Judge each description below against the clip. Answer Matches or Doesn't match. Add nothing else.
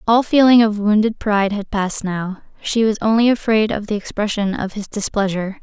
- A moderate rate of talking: Matches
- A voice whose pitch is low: Doesn't match